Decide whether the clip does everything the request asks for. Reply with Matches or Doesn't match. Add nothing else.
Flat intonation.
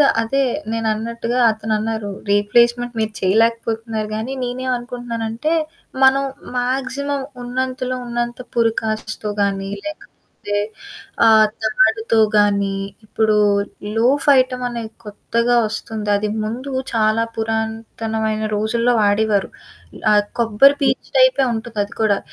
Matches